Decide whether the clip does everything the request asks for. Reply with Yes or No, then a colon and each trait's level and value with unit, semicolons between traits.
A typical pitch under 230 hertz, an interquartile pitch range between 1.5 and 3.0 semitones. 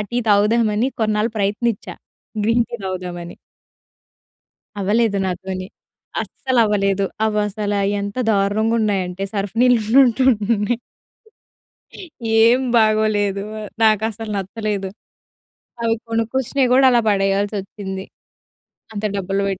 Yes: high, 210 Hz; narrow, 2.4 semitones